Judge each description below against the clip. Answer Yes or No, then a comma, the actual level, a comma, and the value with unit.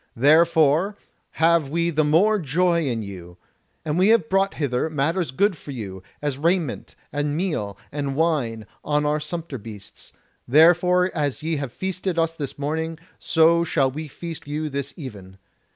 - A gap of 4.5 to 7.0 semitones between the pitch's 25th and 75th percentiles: No, average, 3.6 semitones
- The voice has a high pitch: No, medium, 155 Hz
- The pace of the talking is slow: No, average, 160 wpm